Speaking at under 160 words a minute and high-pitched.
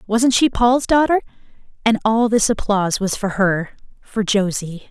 Yes: average, 145 wpm; high, 220 Hz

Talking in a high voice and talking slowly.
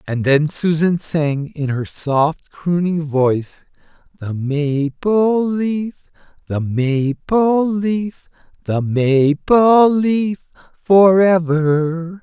No: medium, 165 Hz; slow, 100 wpm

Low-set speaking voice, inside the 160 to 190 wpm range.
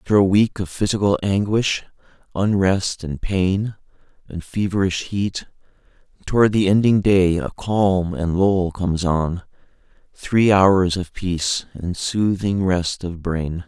No: very low, 95 Hz; slow, 135 wpm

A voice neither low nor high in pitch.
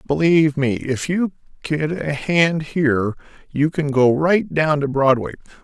Yes: medium, 150 Hz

